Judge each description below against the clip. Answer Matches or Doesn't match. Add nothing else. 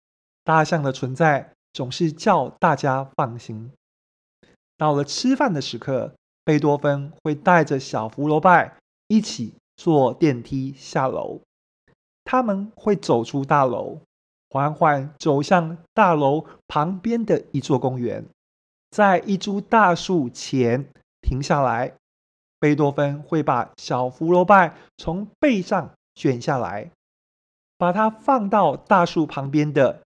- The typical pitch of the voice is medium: Matches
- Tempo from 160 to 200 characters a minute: Matches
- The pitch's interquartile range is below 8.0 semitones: Matches